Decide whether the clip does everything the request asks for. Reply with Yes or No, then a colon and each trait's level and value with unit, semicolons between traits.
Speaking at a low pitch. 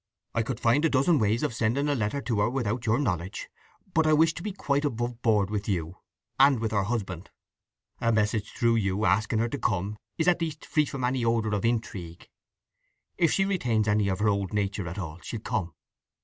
Yes: low, 115 Hz